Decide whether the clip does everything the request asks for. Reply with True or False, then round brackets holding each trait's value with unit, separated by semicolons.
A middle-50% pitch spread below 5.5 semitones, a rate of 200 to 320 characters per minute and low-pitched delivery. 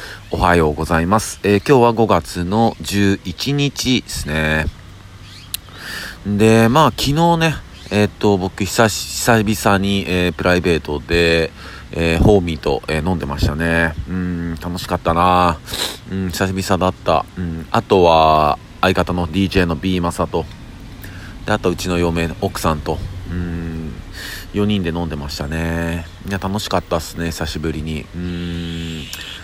True (2.9 semitones; 270 characters per minute; 90 Hz)